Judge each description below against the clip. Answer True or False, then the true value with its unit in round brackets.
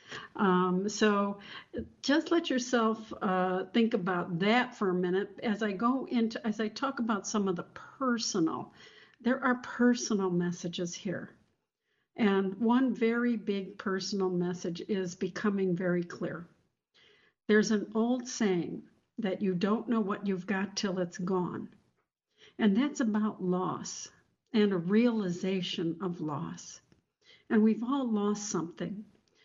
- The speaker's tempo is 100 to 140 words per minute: True (135 wpm)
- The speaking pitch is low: False (205 Hz)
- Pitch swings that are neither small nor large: True (4.0 semitones)